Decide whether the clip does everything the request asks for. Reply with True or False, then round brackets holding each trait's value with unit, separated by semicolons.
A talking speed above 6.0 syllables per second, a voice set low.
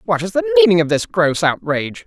False (6.2 syllables/s; 155 Hz)